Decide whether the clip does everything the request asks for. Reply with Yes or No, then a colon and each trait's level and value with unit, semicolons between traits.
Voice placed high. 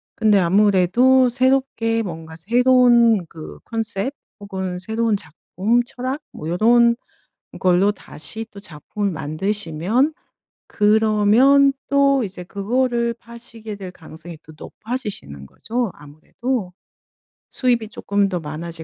Yes: high, 210 Hz